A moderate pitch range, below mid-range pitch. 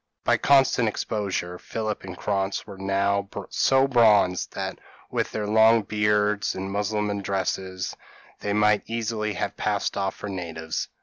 No: narrow, 1.8 semitones; low, 105 Hz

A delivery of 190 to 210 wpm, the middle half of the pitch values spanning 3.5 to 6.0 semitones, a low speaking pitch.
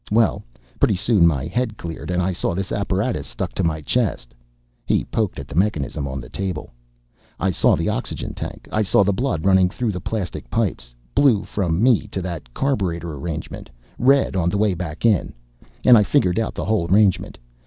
Yes: average, 195 wpm; average, 4.5 semitones; very low, 95 Hz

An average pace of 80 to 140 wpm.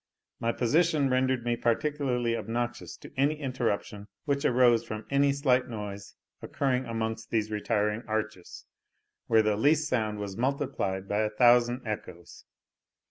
Yes: slow, 135 wpm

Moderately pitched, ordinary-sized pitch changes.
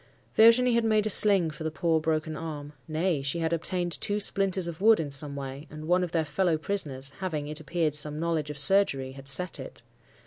Yes: medium, 160 Hz; average, 4.1 semitones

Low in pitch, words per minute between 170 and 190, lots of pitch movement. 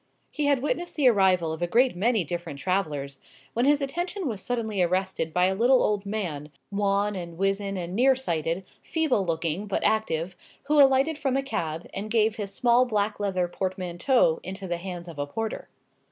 No: high, 195 Hz; average, 185 wpm; wide, 5.9 semitones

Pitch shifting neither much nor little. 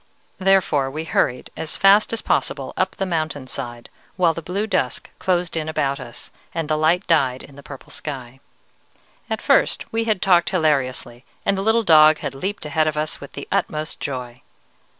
Yes: average, 5.0 semitones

